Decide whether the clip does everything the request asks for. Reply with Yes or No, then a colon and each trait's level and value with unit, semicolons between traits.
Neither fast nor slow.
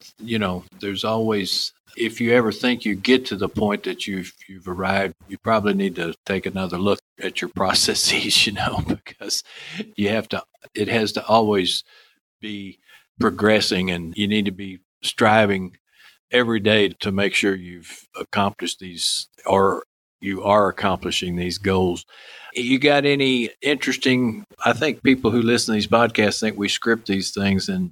Yes: average, 165 wpm